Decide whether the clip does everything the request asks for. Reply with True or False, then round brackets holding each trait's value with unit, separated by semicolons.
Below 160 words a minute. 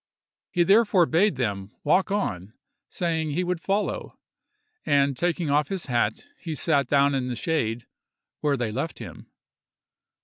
True (145 wpm)